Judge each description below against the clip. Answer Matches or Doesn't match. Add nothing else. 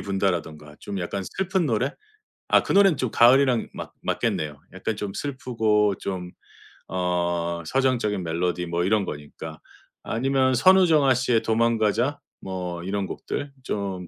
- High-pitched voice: Doesn't match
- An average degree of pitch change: Doesn't match